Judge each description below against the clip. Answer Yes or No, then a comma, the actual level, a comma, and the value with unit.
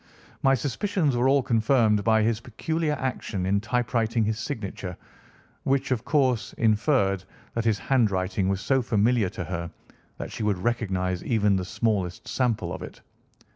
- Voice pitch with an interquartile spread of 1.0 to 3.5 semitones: No, average, 4.3 semitones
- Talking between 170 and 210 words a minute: No, average, 155 wpm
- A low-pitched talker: Yes, low, 110 Hz